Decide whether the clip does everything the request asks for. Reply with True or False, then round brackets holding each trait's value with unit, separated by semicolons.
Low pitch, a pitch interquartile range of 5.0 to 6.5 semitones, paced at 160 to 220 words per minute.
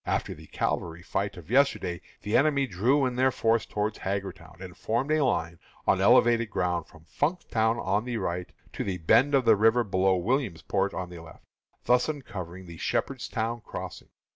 True (105 Hz; 5.6 semitones; 175 wpm)